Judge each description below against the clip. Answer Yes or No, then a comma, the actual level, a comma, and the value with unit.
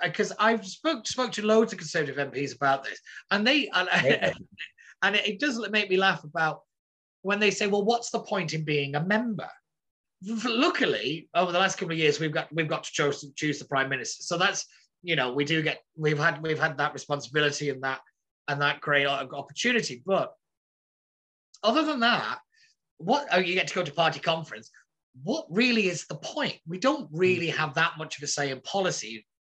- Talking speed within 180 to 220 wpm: Yes, average, 200 wpm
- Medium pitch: Yes, medium, 170 Hz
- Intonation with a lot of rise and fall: Yes, wide, 6.4 semitones